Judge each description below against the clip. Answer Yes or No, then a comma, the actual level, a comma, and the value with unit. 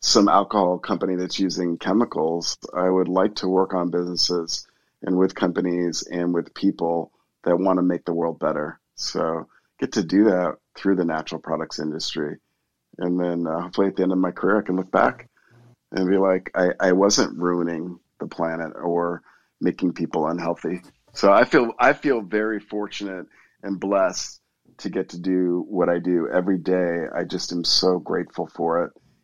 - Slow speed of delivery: No, average, 180 wpm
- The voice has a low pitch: Yes, very low, 90 Hz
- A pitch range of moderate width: No, narrow, 1.6 semitones